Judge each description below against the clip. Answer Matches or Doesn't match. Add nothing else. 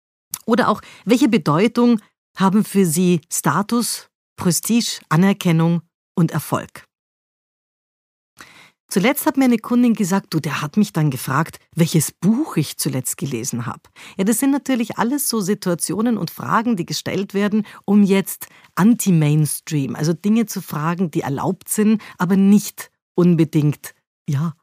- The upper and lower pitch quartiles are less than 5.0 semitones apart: Doesn't match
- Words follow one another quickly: Doesn't match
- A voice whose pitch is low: Doesn't match